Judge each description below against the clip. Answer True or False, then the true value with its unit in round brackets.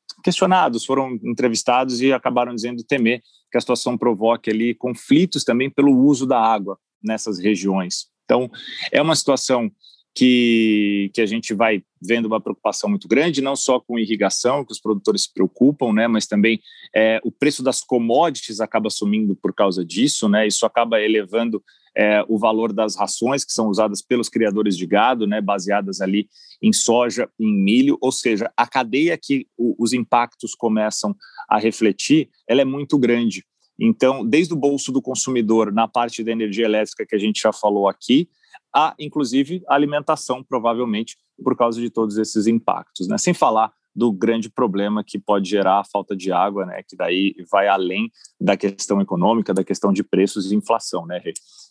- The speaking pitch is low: True (115 Hz)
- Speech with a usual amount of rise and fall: True (3.2 semitones)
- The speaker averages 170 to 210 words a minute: True (175 wpm)